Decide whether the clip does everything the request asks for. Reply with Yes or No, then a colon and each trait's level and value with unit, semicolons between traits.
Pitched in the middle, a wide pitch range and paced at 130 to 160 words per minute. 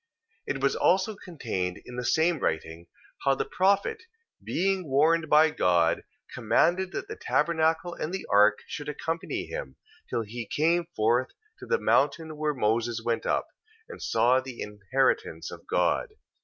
Yes: medium, 150 Hz; wide, 6.6 semitones; average, 155 wpm